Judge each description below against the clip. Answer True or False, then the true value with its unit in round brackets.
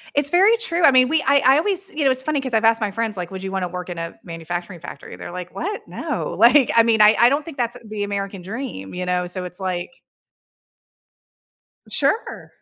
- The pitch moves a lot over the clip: True (7.4 semitones)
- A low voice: False (225 Hz)